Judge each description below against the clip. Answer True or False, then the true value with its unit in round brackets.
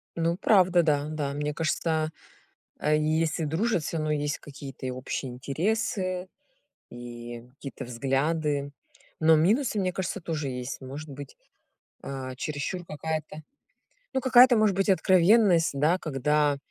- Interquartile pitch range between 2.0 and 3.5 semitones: False (4.3 semitones)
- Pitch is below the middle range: False (155 Hz)